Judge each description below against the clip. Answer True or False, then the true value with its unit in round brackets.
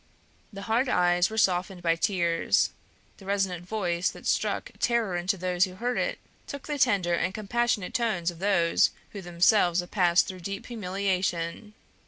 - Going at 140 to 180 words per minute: True (165 wpm)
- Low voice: False (185 Hz)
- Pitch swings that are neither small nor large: True (3.3 semitones)